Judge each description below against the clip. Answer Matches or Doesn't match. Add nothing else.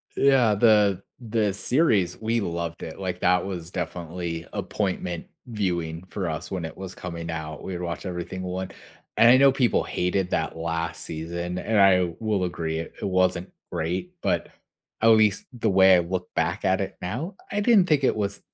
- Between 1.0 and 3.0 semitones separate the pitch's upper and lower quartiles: Doesn't match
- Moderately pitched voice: Doesn't match